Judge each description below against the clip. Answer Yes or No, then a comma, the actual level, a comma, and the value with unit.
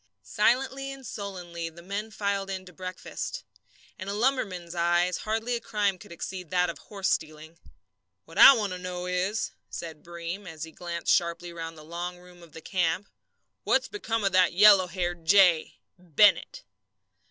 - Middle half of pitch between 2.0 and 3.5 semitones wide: Yes, average, 3.0 semitones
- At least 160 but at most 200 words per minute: Yes, average, 170 wpm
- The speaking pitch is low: No, medium, 180 Hz